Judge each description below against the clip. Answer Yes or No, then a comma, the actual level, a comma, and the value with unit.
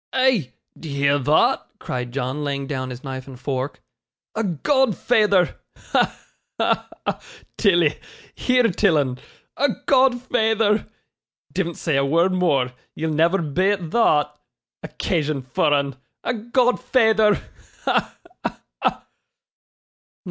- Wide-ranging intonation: Yes, wide, 7.8 semitones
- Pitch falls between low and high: Yes, medium, 165 Hz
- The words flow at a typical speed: No, slow, 120 wpm